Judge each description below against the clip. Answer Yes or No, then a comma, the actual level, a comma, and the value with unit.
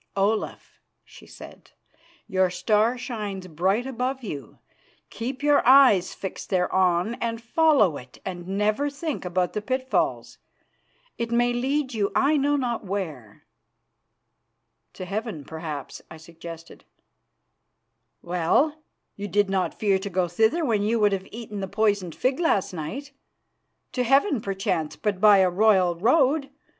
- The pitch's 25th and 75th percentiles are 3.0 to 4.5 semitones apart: No, wide, 5.5 semitones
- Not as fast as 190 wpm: Yes, average, 140 wpm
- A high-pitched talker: Yes, high, 210 Hz